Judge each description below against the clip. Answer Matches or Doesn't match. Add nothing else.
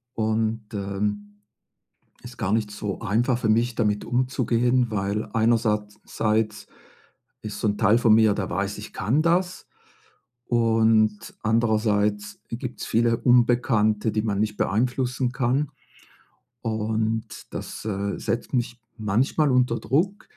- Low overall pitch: Matches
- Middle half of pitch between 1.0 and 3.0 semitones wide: Matches